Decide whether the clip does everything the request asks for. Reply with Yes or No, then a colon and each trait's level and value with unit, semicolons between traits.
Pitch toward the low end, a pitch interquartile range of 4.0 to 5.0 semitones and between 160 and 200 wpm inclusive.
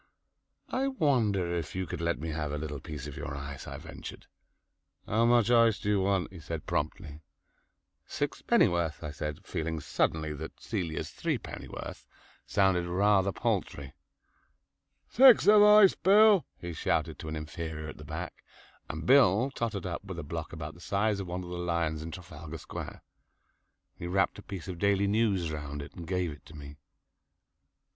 Yes: very low, 85 Hz; average, 4.5 semitones; average, 170 wpm